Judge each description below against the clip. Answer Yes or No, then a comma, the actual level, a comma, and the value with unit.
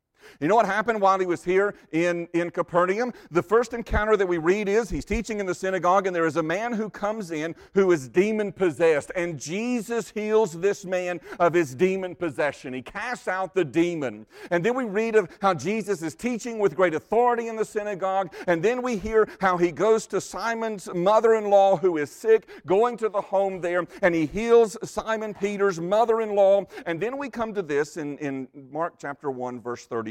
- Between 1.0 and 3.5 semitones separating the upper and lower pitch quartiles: No, average, 4.0 semitones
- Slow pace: No, average, 200 wpm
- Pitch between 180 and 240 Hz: Yes, high, 190 Hz